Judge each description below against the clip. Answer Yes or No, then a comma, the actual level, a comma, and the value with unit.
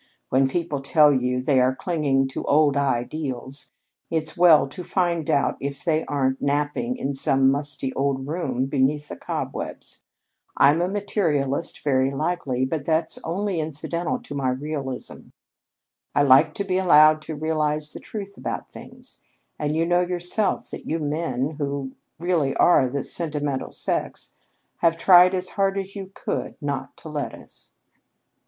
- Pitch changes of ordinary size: Yes, average, 3.9 semitones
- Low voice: No, medium, 150 Hz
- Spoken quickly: No, average, 155 wpm